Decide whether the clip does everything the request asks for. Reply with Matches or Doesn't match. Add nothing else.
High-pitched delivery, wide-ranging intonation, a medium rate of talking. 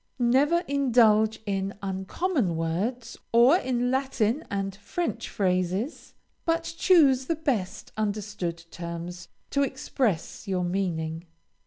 Doesn't match